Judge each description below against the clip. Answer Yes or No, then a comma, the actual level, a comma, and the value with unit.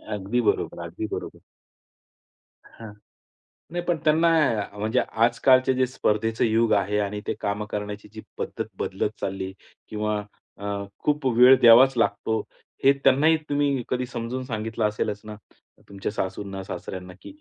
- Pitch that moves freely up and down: No, average, 3.8 semitones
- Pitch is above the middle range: No, low, 110 Hz